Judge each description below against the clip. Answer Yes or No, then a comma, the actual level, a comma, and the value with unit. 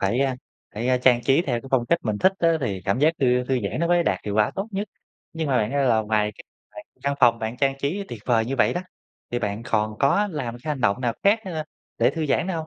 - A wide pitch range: Yes, wide, 5.7 semitones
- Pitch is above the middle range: No, low, 130 Hz